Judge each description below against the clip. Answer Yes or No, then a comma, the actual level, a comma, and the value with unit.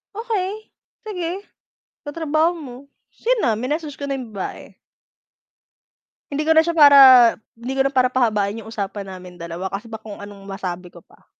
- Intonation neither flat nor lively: No, wide, 8.1 semitones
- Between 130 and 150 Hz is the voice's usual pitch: No, very high, 250 Hz